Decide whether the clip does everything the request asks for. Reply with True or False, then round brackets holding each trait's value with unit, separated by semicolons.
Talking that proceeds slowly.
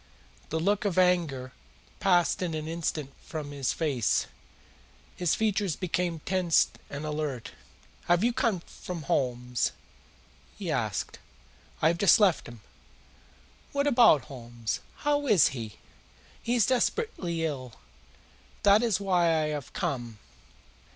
True (130 wpm)